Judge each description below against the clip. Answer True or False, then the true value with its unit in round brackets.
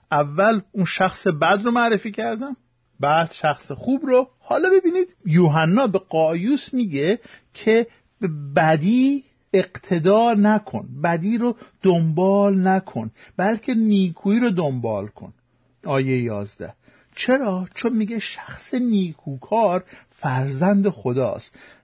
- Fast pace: False (110 wpm)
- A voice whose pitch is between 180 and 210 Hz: True (190 Hz)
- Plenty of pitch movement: True (6.2 semitones)